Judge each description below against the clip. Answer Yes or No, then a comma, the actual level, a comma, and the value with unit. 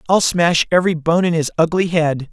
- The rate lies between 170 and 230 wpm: Yes, fast, 205 wpm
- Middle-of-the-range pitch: Yes, medium, 165 Hz